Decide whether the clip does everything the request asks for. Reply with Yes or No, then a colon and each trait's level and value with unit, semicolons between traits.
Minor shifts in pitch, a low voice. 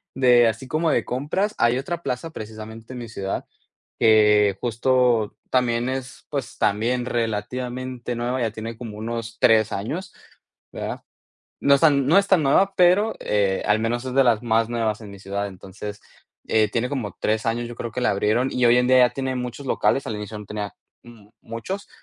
No: average, 3.1 semitones; low, 120 Hz